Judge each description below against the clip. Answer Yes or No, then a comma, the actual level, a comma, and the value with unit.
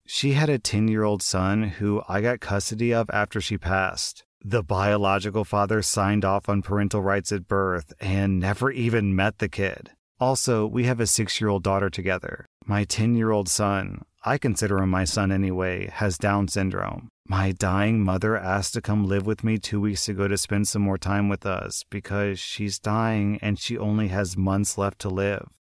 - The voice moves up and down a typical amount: No, narrow, 1.9 semitones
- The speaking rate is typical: Yes, average, 195 wpm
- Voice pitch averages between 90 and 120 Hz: Yes, low, 100 Hz